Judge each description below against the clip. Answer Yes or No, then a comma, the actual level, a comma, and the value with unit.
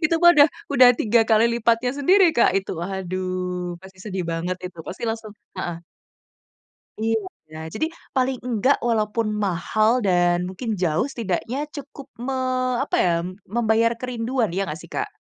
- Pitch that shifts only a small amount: No, average, 5.1 semitones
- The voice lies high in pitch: Yes, high, 220 Hz